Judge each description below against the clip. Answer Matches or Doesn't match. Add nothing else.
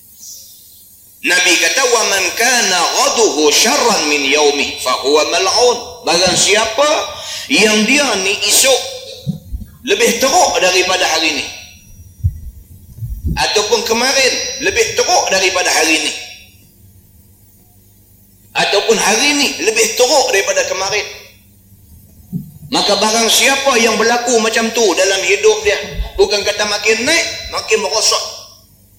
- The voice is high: Matches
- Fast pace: Doesn't match